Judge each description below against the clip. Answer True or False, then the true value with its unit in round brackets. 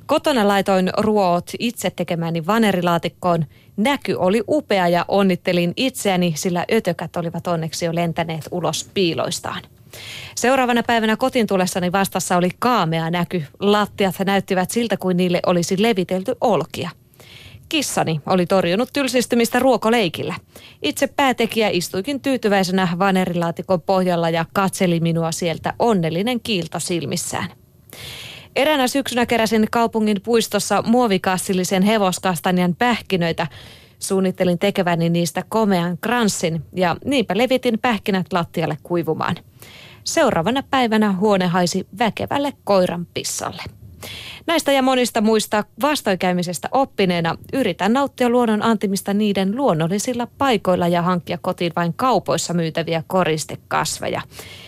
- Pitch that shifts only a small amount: False (4.7 semitones)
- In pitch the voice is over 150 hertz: True (190 Hz)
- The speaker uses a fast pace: False (110 wpm)